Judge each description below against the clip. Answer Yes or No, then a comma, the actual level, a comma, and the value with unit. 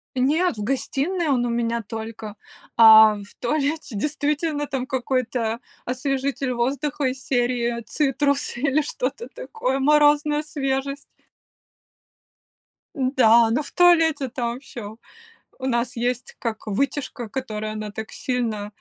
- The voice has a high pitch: Yes, very high, 255 Hz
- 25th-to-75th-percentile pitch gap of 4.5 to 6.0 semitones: No, average, 3.6 semitones